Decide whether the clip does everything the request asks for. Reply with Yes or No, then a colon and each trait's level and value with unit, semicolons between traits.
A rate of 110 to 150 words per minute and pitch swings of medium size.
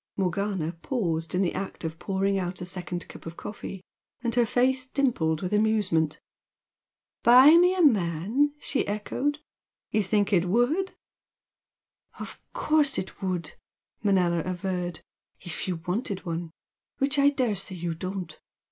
No: average, 140 wpm; wide, 5.7 semitones